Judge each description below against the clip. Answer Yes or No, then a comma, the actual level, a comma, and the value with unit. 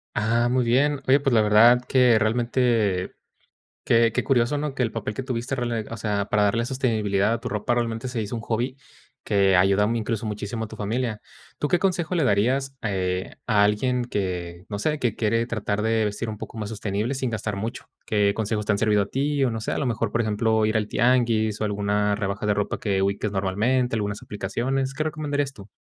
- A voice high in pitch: No, low, 110 Hz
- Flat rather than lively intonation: No, average, 3.2 semitones